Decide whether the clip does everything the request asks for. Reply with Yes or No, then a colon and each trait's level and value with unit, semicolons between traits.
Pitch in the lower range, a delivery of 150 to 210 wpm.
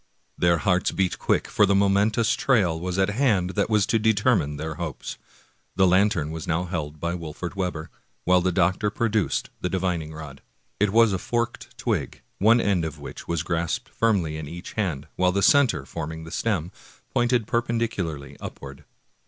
Yes: very low, 90 Hz; average, 175 wpm